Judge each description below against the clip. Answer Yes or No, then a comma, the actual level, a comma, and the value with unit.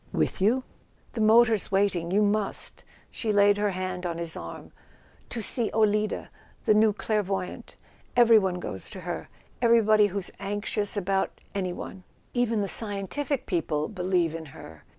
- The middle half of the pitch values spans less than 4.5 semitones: Yes, average, 2.9 semitones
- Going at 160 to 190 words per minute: No, average, 150 wpm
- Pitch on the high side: Yes, high, 205 Hz